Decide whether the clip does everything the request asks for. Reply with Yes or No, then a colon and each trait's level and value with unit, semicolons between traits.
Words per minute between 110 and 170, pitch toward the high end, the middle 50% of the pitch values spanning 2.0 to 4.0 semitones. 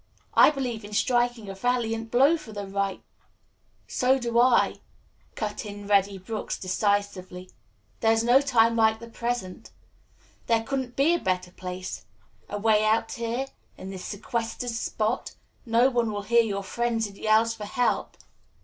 Yes: average, 155 wpm; high, 225 Hz; average, 2.9 semitones